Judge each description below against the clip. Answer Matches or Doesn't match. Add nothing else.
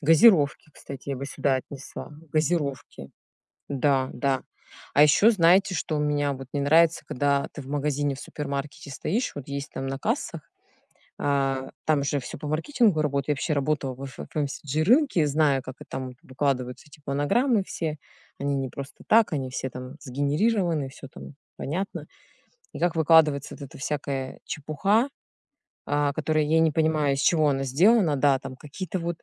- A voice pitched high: Doesn't match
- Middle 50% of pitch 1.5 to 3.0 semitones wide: Matches